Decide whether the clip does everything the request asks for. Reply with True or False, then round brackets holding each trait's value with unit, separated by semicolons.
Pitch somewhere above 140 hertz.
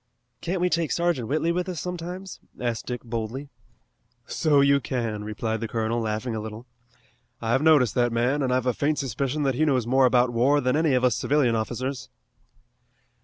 False (130 Hz)